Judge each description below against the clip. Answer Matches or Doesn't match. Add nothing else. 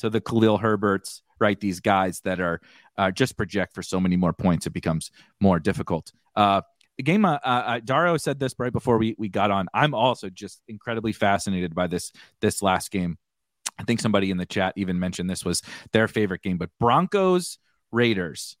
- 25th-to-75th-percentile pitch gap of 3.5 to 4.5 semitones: Matches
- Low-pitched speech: Matches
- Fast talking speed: Doesn't match